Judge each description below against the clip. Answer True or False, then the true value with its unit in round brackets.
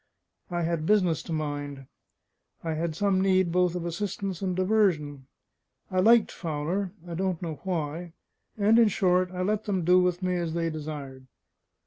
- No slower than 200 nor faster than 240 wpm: False (165 wpm)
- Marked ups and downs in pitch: False (3.0 semitones)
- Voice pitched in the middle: True (180 Hz)